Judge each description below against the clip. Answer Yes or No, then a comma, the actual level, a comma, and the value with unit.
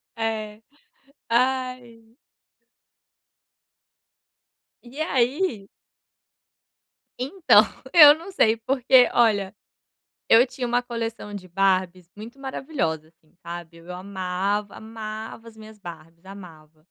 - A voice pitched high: Yes, high, 220 Hz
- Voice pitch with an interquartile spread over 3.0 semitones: Yes, average, 4.8 semitones